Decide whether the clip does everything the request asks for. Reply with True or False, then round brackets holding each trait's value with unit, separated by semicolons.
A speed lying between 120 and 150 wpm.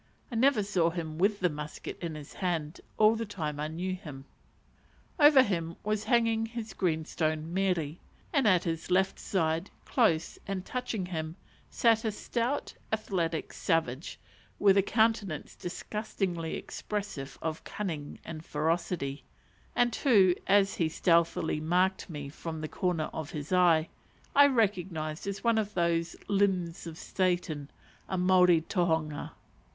True (145 wpm)